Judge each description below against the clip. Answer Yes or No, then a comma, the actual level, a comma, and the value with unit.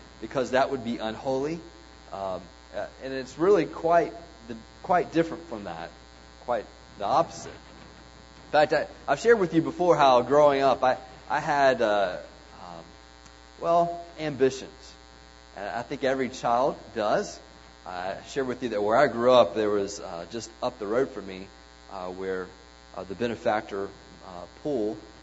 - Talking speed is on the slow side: No, average, 160 wpm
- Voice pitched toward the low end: Yes, low, 100 Hz